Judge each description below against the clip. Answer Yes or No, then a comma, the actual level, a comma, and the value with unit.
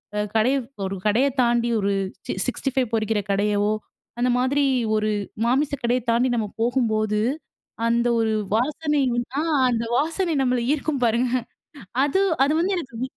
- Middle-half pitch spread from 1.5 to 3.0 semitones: No, average, 3.8 semitones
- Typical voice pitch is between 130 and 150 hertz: No, high, 240 Hz